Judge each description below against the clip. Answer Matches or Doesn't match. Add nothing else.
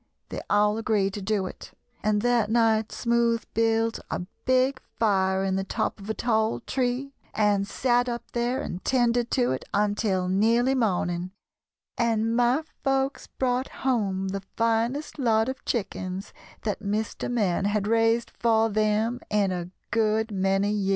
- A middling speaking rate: Matches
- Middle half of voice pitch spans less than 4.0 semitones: Matches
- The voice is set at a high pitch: Matches